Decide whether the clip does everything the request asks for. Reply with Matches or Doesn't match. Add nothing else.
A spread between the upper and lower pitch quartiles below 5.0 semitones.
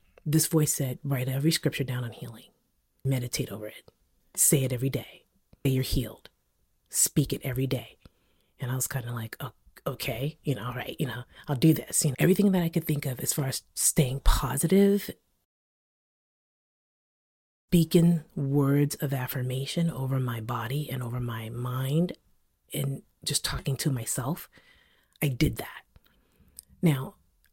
Matches